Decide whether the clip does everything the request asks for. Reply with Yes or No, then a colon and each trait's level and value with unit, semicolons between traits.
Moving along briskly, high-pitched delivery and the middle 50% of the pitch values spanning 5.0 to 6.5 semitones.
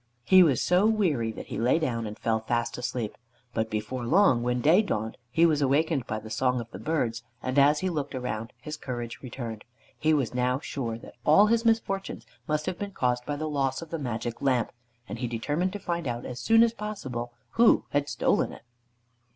No: fast, 210 wpm; low, 130 Hz; wide, 5.6 semitones